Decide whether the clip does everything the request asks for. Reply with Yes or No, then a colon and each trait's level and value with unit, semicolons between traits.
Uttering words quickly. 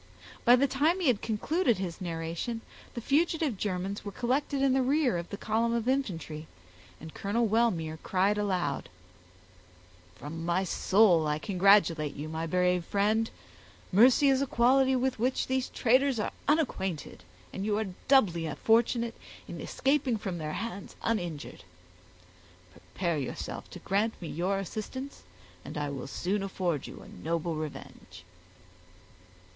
No: average, 145 wpm